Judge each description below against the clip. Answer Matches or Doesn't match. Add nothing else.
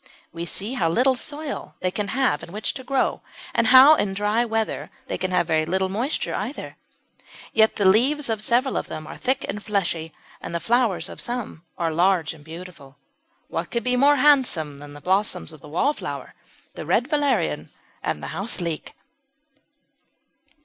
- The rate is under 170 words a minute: Doesn't match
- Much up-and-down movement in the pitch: Matches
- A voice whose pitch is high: Matches